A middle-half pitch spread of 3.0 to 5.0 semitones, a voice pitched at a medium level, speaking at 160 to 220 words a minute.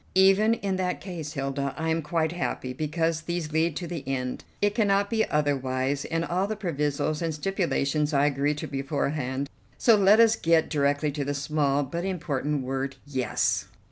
Yes: average, 4.0 semitones; medium, 155 Hz; average, 175 wpm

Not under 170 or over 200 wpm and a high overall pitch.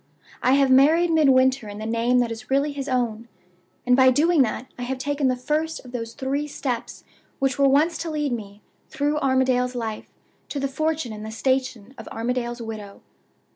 Yes: average, 190 wpm; very high, 260 Hz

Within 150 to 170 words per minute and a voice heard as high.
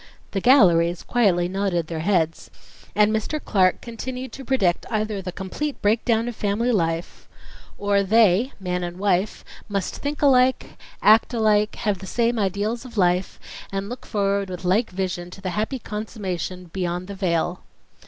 Yes: average, 160 wpm; high, 200 Hz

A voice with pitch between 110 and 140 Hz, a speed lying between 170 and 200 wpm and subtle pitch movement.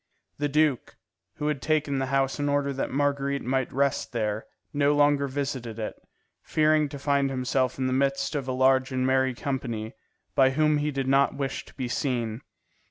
Yes: low, 135 Hz; average, 185 wpm; narrow, 1.8 semitones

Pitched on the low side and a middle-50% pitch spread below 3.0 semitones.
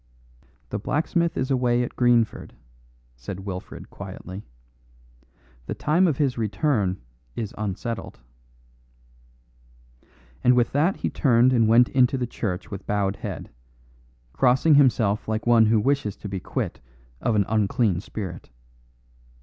No: low, 115 Hz; average, 4.0 semitones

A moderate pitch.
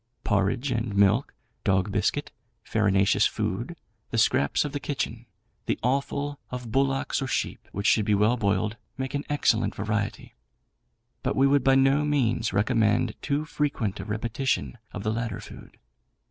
No: low, 115 Hz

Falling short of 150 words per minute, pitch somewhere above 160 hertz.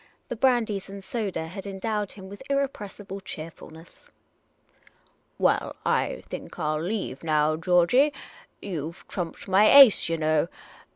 Yes: average, 140 wpm; high, 190 Hz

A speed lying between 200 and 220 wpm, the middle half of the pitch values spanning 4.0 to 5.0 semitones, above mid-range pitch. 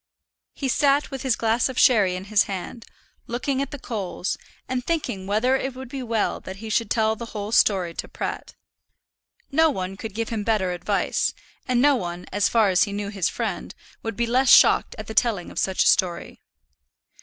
Yes: fast, 205 wpm; average, 4.4 semitones; high, 225 Hz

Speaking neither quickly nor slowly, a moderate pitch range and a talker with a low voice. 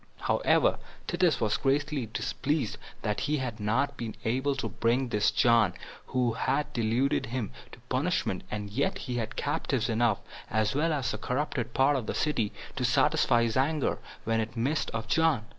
Yes: average, 170 wpm; average, 4.1 semitones; low, 125 Hz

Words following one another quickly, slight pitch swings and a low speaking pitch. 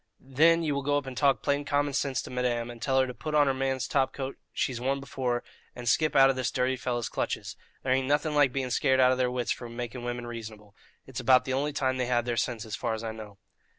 Yes: fast, 265 wpm; narrow, 2.2 semitones; low, 130 Hz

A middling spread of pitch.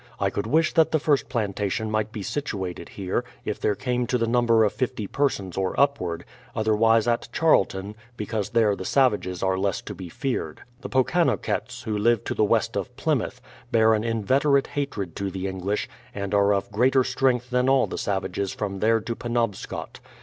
Yes: average, 4.1 semitones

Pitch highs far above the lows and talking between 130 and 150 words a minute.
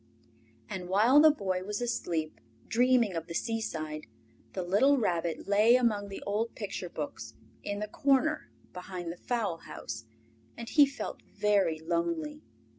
Yes: wide, 5.9 semitones; average, 145 wpm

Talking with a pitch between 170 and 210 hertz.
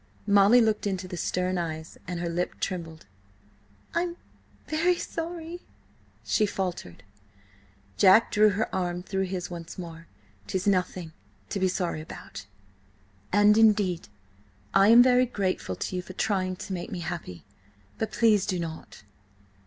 Yes: medium, 185 Hz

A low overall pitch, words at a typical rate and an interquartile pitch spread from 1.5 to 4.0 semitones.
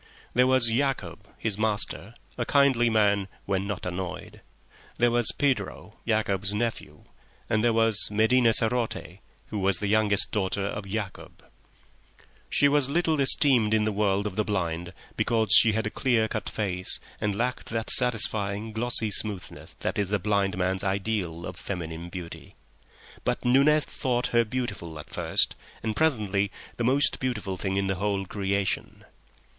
Yes: low, 105 Hz; average, 155 wpm; average, 3.3 semitones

